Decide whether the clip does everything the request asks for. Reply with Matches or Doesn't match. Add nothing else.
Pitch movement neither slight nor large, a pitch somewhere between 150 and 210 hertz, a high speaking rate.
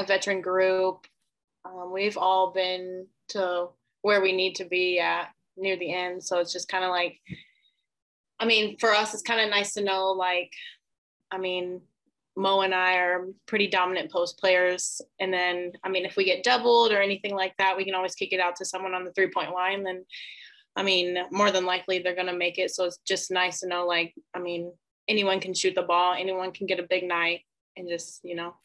Doesn't match